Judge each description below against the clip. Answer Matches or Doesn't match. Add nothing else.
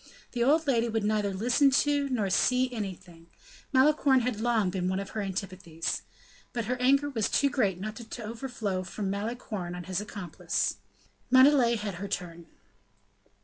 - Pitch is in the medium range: Doesn't match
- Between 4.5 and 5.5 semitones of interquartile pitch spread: Matches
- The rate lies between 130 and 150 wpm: Doesn't match